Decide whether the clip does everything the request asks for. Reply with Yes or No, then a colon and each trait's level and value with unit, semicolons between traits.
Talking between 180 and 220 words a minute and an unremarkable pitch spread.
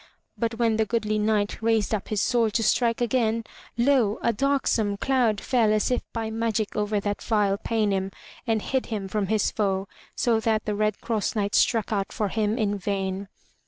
No: average, 185 wpm; narrow, 2.0 semitones